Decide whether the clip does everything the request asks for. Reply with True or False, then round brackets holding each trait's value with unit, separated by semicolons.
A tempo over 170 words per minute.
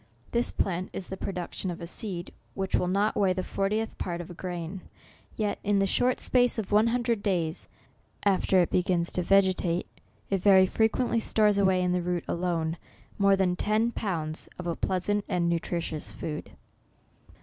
True (180 wpm)